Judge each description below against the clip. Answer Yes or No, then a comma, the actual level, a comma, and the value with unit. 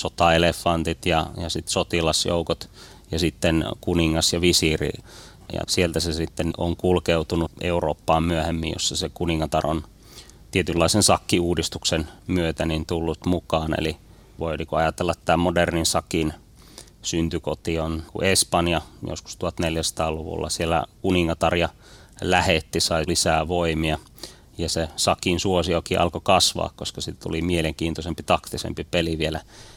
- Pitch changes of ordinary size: No, narrow, 1.6 semitones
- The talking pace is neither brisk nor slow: Yes, average, 120 wpm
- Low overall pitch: Yes, very low, 85 Hz